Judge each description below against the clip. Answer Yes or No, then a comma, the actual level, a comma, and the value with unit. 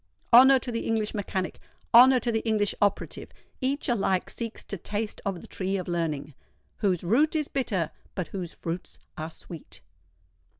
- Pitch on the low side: No, high, 205 Hz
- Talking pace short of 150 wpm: No, average, 160 wpm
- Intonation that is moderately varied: Yes, average, 4.8 semitones